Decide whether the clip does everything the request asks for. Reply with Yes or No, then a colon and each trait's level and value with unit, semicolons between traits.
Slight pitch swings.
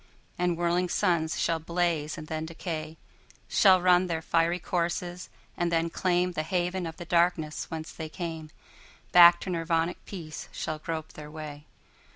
Yes: narrow, 1.9 semitones